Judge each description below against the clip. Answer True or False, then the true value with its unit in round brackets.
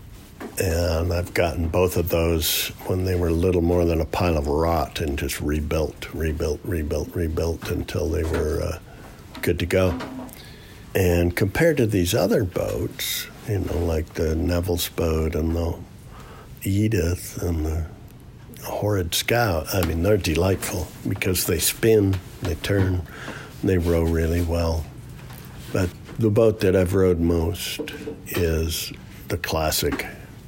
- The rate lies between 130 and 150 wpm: True (140 wpm)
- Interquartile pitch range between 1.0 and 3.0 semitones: True (2.6 semitones)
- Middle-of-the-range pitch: False (85 Hz)